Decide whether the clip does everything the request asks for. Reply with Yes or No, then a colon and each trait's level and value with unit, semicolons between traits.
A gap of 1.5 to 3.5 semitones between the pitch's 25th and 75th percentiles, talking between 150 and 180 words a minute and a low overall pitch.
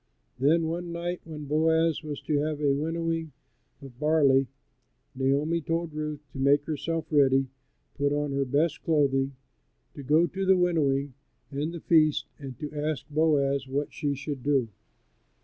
No: average, 2.7 semitones; average, 160 wpm; medium, 150 Hz